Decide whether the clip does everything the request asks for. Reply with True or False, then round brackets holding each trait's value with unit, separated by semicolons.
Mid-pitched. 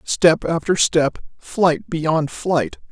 True (165 Hz)